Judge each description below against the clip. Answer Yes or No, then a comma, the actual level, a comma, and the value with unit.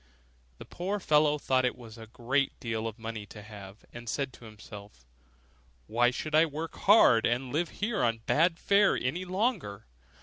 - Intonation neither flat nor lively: No, wide, 6.6 semitones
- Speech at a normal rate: Yes, average, 175 wpm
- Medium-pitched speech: No, low, 125 Hz